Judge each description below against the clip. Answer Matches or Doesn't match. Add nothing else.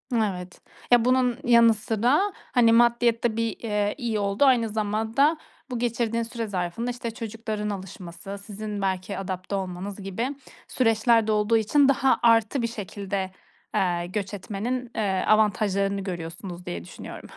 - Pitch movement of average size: Matches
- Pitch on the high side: Matches